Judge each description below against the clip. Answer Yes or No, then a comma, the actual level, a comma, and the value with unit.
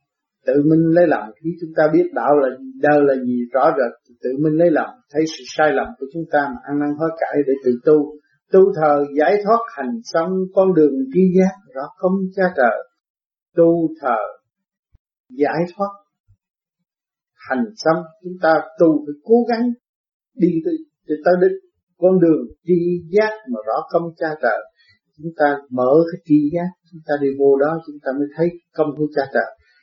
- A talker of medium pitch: Yes, medium, 165 Hz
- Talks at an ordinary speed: Yes, average, 185 wpm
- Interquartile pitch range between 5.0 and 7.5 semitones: No, average, 4.0 semitones